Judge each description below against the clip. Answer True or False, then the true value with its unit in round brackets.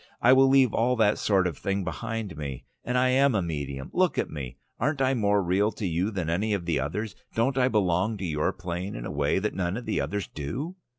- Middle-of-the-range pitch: False (100 Hz)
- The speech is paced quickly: True (240 wpm)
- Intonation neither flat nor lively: False (5.7 semitones)